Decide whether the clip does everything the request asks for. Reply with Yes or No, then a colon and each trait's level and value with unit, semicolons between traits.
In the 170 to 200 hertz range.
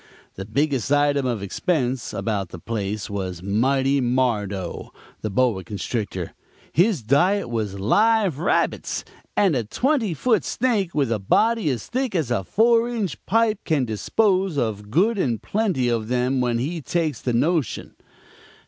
No: low, 130 Hz